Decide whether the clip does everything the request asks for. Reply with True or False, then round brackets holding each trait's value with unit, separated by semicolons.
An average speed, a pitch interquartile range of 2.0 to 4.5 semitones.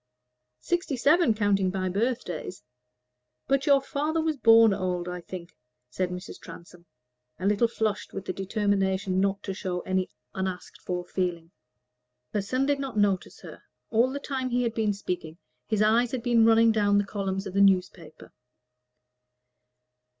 True (155 wpm; 3.9 semitones)